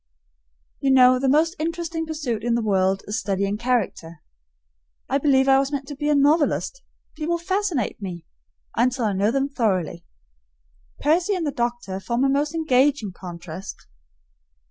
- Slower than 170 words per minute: Yes, average, 155 wpm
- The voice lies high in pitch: Yes, very high, 265 Hz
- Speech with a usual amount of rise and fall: No, wide, 6.4 semitones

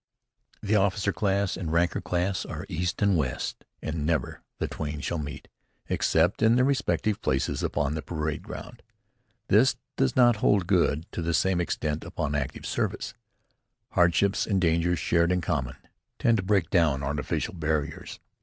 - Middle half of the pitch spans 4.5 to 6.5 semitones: No, average, 4.1 semitones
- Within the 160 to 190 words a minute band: Yes, average, 165 wpm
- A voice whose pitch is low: Yes, very low, 85 Hz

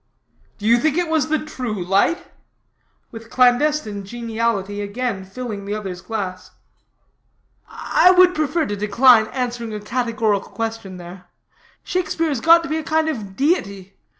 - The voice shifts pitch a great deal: Yes, wide, 6.7 semitones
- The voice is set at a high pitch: Yes, high, 230 Hz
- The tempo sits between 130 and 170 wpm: Yes, average, 150 wpm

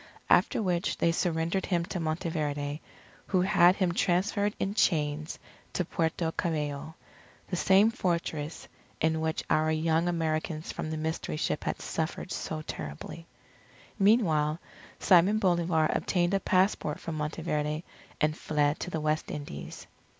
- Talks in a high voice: No, medium, 160 Hz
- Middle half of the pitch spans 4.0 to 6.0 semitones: No, narrow, 2.6 semitones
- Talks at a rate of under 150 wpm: Yes, slow, 135 wpm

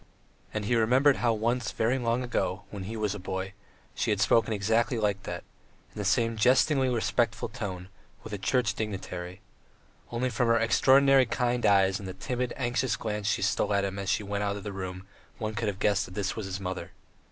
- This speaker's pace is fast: Yes, fast, 210 wpm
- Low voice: Yes, low, 110 Hz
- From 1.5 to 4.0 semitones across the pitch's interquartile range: Yes, average, 3.4 semitones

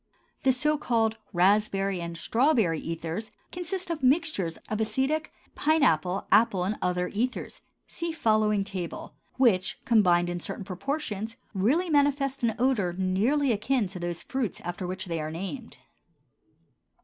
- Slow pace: No, average, 150 wpm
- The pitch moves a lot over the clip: Yes, wide, 6.8 semitones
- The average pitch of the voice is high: Yes, high, 215 Hz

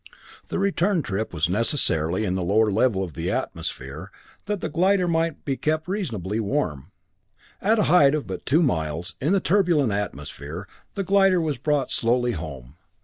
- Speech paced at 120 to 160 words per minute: No, average, 170 wpm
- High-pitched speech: No, low, 125 Hz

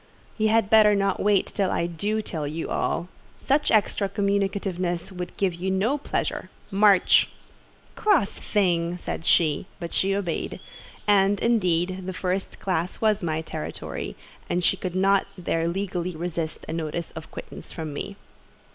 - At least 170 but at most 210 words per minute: No, average, 155 wpm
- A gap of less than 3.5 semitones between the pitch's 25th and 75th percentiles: Yes, average, 2.9 semitones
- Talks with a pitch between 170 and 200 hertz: Yes, medium, 185 Hz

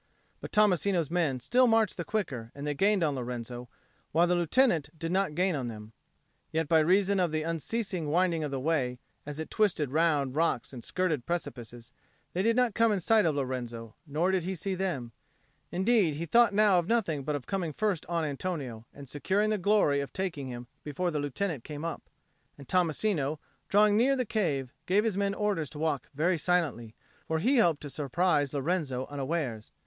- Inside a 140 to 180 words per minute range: No, average, 195 wpm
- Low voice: No, medium, 165 Hz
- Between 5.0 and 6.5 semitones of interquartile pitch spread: Yes, average, 5.3 semitones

